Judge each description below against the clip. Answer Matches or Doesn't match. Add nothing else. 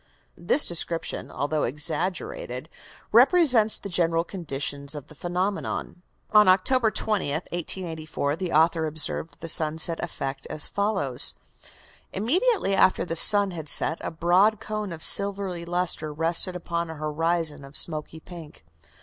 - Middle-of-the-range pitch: Matches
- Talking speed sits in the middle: Doesn't match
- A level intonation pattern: Doesn't match